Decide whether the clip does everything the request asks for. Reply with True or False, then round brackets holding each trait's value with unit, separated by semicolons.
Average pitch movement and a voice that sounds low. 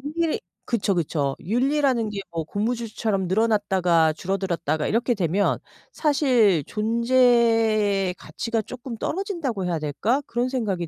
False (4.8 semitones; 215 Hz)